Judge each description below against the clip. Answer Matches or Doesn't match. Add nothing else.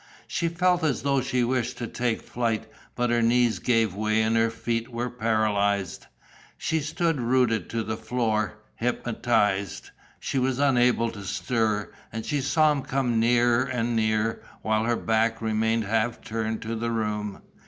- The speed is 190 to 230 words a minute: Doesn't match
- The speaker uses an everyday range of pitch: Doesn't match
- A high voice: Doesn't match